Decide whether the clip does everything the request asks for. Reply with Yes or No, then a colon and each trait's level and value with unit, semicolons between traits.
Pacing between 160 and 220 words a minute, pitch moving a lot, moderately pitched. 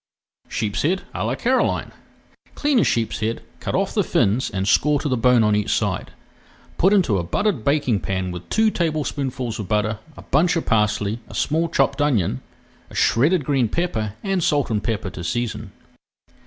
No: average, 175 wpm; wide, 6.5 semitones; low, 120 Hz